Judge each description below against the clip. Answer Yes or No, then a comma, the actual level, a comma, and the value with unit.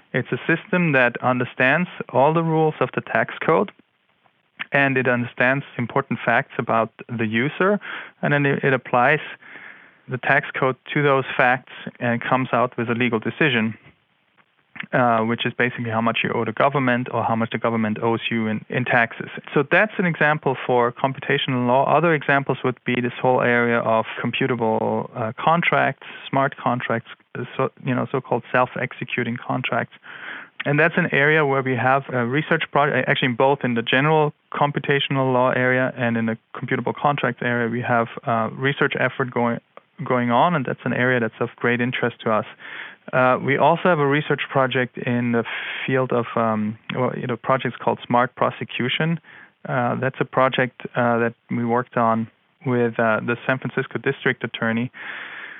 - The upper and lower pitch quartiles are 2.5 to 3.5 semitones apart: Yes, average, 2.8 semitones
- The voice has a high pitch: No, low, 125 Hz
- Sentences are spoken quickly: No, average, 175 wpm